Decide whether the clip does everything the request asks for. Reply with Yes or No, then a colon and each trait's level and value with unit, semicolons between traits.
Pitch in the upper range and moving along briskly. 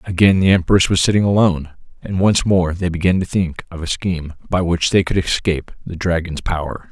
No: very low, 90 Hz; fast, 210 wpm